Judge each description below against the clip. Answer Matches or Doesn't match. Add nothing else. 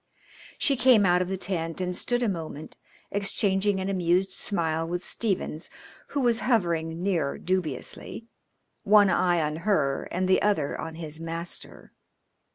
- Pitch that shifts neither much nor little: Matches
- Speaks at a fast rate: Doesn't match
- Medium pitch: Matches